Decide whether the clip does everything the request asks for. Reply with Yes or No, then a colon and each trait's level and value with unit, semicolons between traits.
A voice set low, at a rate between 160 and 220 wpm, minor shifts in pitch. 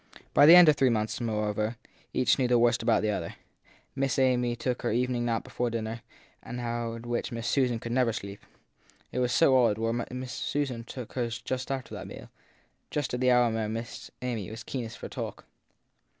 Yes: low, 120 Hz; average, 200 wpm; narrow, 1.8 semitones